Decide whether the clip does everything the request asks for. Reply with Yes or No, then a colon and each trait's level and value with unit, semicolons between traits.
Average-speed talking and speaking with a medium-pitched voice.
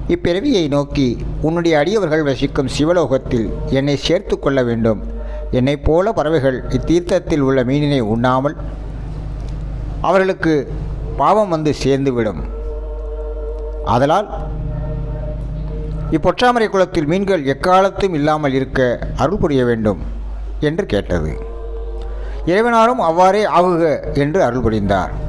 Yes: average, 95 wpm; medium, 150 Hz